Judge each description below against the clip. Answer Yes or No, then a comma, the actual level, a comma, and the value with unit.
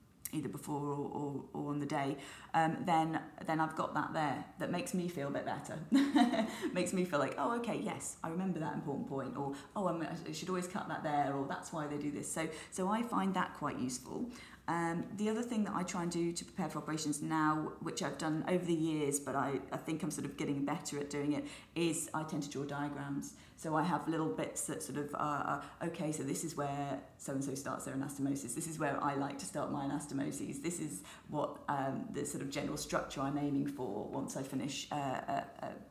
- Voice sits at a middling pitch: Yes, medium, 155 Hz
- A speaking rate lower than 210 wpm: No, fast, 235 wpm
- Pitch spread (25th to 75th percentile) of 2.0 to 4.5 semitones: Yes, average, 3.0 semitones